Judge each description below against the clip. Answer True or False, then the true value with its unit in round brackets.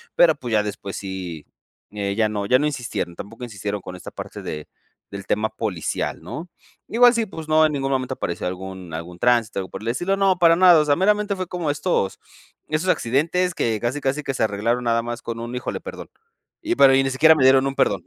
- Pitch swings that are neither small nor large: False (7.3 semitones)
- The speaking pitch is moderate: False (125 Hz)